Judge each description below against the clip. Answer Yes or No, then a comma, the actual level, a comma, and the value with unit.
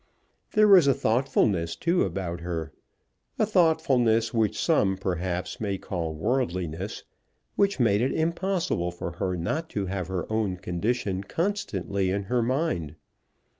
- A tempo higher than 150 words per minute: No, slow, 135 wpm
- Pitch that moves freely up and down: Yes, wide, 7.6 semitones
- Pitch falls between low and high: No, low, 100 Hz